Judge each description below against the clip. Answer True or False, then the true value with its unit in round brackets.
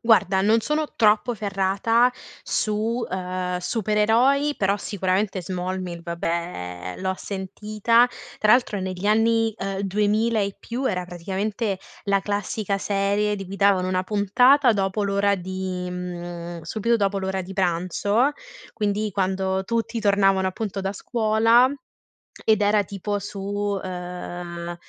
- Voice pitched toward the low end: False (200 Hz)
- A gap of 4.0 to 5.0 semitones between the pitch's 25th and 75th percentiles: False (2.5 semitones)